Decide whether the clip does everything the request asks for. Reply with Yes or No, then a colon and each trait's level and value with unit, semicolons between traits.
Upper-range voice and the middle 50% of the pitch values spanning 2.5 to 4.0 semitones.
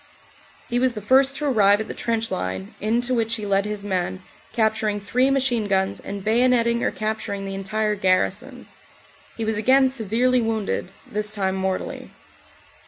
Yes: high, 215 Hz; average, 3.2 semitones